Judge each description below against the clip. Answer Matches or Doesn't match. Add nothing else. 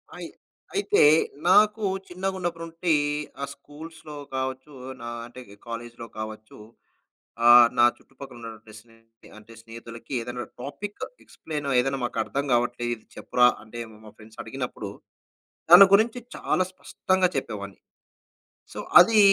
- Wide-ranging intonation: Matches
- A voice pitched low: Matches